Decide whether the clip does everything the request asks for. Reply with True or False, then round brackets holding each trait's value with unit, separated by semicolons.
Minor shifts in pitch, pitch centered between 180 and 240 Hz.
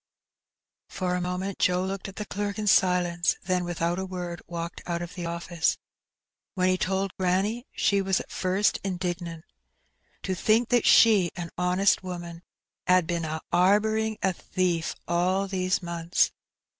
True (2.0 semitones; 185 Hz)